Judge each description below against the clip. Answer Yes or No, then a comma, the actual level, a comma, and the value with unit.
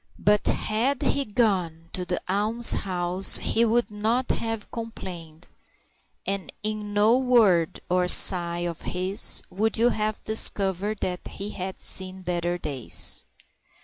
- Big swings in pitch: No, average, 3.6 semitones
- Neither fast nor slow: No, slow, 130 wpm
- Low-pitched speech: No, high, 200 Hz